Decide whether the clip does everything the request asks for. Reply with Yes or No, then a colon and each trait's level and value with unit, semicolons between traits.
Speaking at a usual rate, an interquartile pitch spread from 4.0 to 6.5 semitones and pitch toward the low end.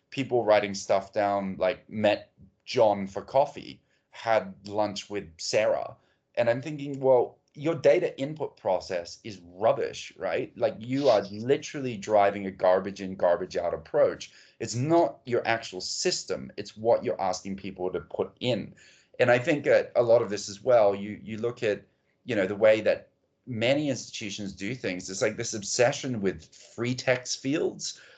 Yes: average, 170 wpm; average, 4.4 semitones; low, 110 Hz